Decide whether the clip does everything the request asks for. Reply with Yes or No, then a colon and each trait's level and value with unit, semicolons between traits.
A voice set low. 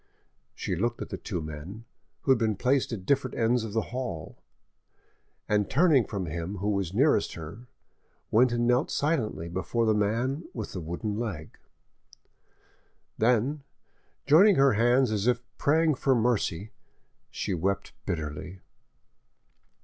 Yes: low, 110 Hz